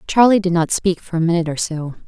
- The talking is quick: Yes, fast, 260 wpm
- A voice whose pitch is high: No, medium, 175 Hz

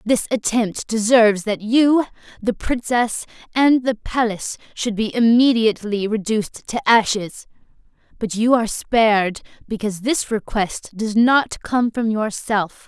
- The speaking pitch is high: Yes, high, 225 Hz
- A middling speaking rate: No, slow, 130 wpm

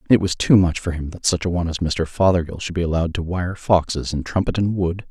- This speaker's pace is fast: Yes, fast, 270 wpm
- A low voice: Yes, very low, 85 Hz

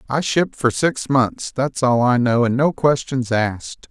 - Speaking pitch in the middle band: No, low, 130 Hz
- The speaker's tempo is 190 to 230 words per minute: Yes, average, 200 wpm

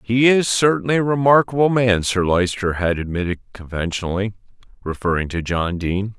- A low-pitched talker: Yes, low, 105 Hz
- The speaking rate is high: No, average, 145 wpm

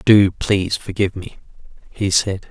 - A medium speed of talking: Yes, average, 145 wpm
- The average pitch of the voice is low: Yes, low, 100 Hz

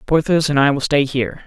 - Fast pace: Yes, fast, 245 wpm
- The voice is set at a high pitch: No, medium, 140 Hz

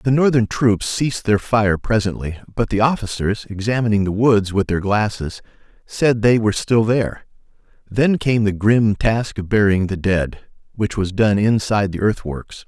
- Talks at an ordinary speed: Yes, average, 170 wpm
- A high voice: No, low, 105 Hz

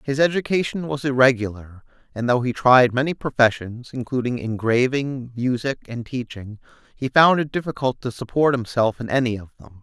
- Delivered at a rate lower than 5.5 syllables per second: Yes, 5.2 syllables/s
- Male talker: Yes, male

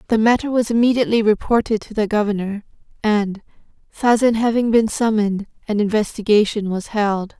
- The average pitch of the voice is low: No, high, 215 Hz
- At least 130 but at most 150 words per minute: Yes, average, 140 wpm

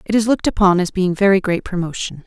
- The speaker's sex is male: No, female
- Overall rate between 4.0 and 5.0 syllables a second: No, 6.5 syllables/s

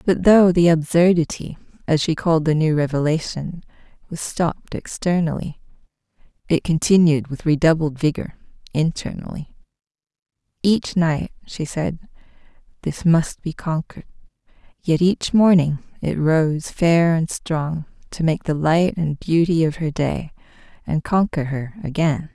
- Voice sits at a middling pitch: Yes, medium, 160 Hz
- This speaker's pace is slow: Yes, slow, 130 wpm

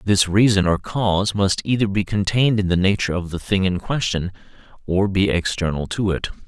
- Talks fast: No, average, 195 wpm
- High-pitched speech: No, very low, 95 Hz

